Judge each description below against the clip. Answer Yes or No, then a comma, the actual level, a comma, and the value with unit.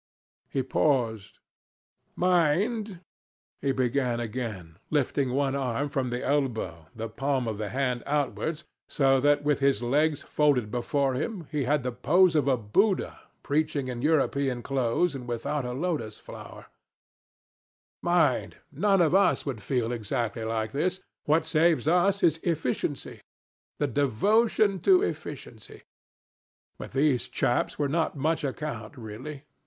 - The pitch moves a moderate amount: Yes, average, 4.3 semitones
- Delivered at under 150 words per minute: Yes, average, 140 wpm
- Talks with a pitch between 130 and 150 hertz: Yes, medium, 140 Hz